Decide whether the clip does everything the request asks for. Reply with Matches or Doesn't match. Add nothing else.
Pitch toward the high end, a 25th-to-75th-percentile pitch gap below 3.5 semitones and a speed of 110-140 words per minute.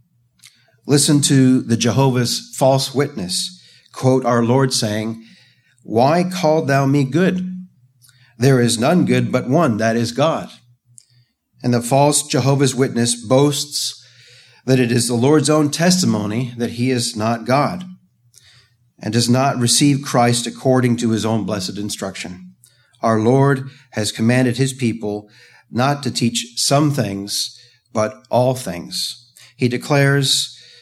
Doesn't match